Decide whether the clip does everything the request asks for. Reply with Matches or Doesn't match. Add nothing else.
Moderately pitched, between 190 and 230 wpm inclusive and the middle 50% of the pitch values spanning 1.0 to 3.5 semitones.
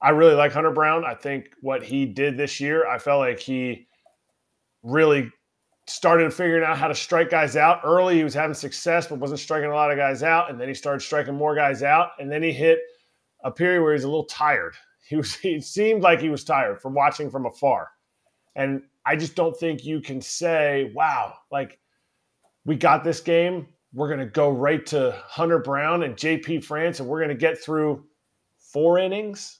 Matches